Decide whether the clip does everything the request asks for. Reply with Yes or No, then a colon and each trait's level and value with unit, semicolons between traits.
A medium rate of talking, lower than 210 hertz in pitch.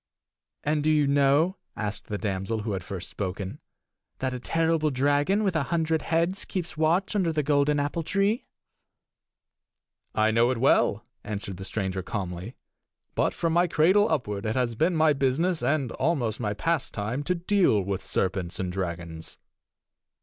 Yes: average, 160 wpm; medium, 140 Hz